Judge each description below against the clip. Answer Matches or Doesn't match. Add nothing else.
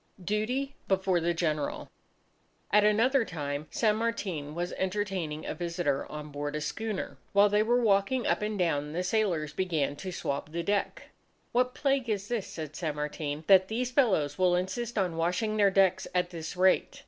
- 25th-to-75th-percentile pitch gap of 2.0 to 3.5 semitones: Doesn't match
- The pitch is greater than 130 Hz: Matches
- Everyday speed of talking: Matches